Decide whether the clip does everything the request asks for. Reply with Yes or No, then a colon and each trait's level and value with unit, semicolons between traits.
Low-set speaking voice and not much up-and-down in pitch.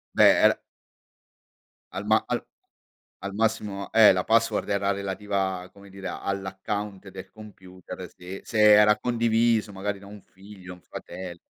Yes: low, 100 Hz; narrow, 1.8 semitones